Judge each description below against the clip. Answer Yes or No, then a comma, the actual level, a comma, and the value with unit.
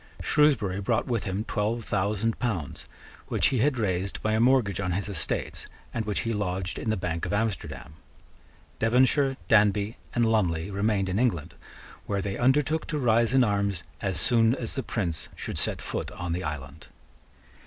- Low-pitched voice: Yes, low, 105 Hz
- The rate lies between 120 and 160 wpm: No, average, 175 wpm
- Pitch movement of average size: Yes, average, 4.0 semitones